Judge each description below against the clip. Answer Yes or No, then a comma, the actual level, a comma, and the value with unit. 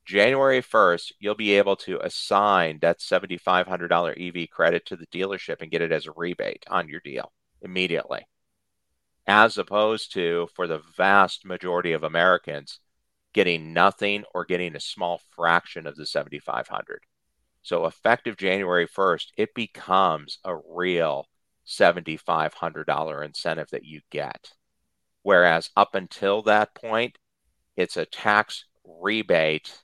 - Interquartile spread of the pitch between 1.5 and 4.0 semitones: Yes, average, 3.2 semitones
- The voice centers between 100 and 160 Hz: No, very low, 90 Hz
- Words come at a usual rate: No, slow, 130 wpm